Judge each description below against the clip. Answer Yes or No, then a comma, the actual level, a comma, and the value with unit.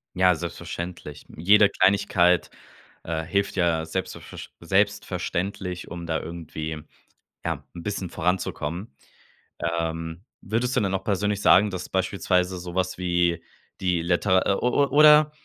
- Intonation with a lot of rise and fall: No, average, 2.7 semitones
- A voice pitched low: Yes, very low, 90 Hz